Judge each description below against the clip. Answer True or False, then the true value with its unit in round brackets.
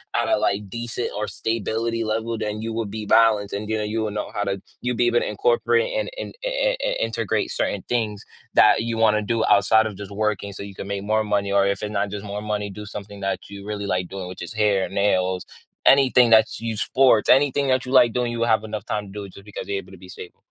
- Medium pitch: False (105 Hz)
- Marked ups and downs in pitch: False (2.5 semitones)